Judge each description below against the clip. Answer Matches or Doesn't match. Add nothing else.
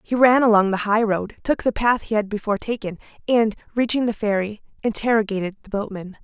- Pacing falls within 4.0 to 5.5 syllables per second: Doesn't match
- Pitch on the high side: Matches